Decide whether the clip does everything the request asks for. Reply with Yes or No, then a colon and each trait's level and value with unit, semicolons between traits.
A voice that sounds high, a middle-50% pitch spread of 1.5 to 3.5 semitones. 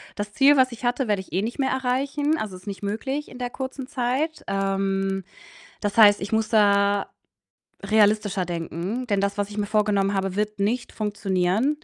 No: high, 210 Hz; average, 4.0 semitones